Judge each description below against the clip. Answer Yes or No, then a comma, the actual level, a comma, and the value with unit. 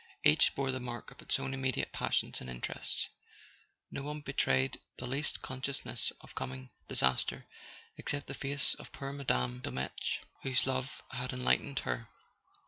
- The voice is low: Yes, low, 130 Hz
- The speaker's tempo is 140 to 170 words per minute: Yes, average, 155 wpm